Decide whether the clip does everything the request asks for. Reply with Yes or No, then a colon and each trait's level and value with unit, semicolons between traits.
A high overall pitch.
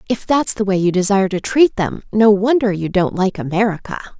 Yes: high, 205 Hz